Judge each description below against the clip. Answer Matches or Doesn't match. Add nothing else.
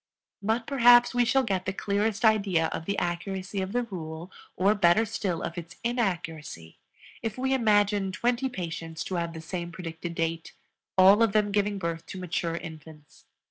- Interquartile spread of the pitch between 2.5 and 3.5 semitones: Doesn't match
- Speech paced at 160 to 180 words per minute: Matches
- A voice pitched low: Doesn't match